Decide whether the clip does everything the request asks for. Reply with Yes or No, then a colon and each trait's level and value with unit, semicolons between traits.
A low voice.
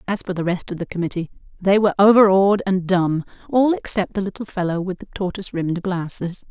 No: high, 190 Hz